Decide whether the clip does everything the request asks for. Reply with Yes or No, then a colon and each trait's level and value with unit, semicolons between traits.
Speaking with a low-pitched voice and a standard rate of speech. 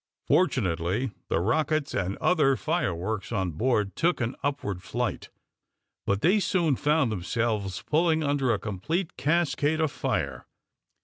No: low, 130 Hz; slow, 130 wpm